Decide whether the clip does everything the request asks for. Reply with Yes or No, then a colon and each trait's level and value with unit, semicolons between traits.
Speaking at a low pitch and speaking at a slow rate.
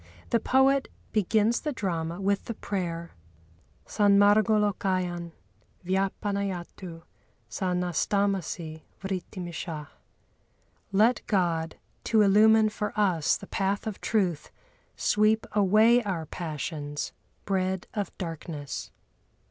No: high, 195 Hz; slow, 90 wpm